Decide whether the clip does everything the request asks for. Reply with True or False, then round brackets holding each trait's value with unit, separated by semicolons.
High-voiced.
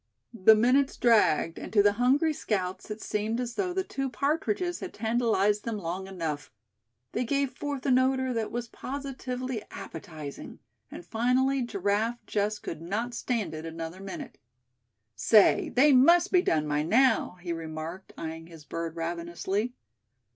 True (220 Hz)